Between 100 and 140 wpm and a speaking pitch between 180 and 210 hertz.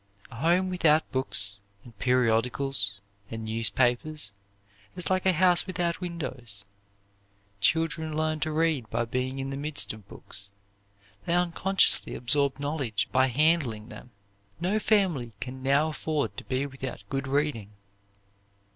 No: slow, 135 wpm; medium, 140 Hz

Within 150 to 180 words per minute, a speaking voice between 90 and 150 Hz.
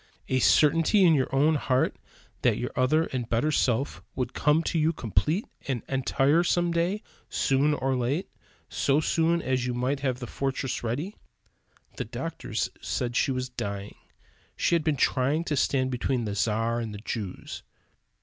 Yes: average, 170 wpm; low, 135 Hz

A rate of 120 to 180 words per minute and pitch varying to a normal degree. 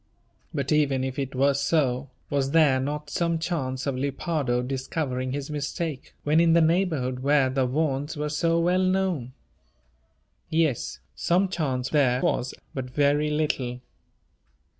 Yes: average, 140 wpm; average, 3.6 semitones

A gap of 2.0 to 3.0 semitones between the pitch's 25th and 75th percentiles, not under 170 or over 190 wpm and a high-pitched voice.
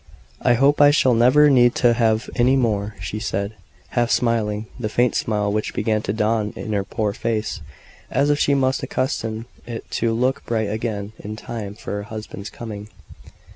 No: narrow, 2.5 semitones; average, 180 wpm; low, 110 Hz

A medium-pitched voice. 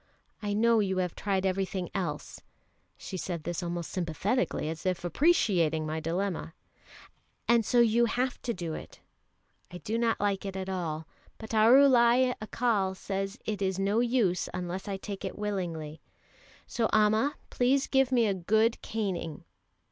No: high, 195 Hz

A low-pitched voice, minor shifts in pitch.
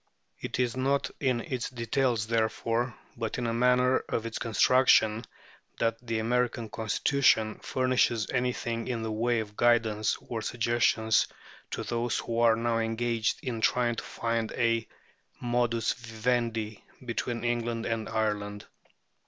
Yes: low, 115 Hz; narrow, 1.4 semitones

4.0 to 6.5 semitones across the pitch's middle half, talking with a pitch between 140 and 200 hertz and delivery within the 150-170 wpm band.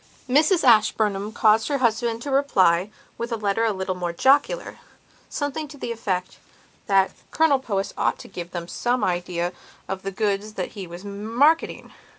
No: average, 5.1 semitones; high, 215 Hz; average, 165 wpm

